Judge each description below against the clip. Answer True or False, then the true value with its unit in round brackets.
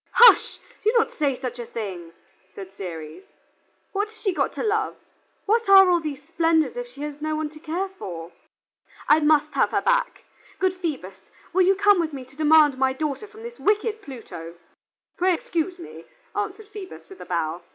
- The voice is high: True (320 Hz)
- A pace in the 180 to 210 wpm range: True (190 wpm)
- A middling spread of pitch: False (6.9 semitones)